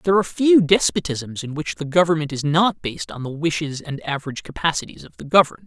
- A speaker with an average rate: No, fast, 210 wpm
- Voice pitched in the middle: Yes, medium, 155 Hz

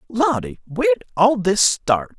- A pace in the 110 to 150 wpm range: Yes, average, 140 wpm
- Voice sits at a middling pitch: Yes, medium, 165 Hz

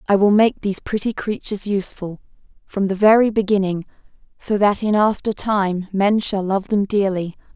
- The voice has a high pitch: Yes, high, 200 Hz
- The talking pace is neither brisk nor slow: Yes, average, 165 wpm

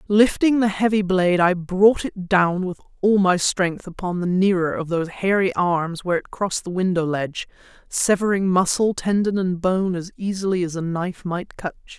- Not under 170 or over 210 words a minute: Yes, average, 190 wpm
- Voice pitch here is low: No, medium, 185 Hz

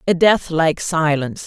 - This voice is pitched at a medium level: Yes, medium, 165 Hz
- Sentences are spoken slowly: Yes, slow, 125 wpm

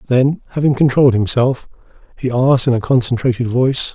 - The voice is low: Yes, low, 125 Hz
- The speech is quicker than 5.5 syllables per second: Yes, 6.1 syllables/s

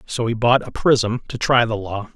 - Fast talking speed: Yes, fast, 250 wpm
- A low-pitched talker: Yes, low, 115 Hz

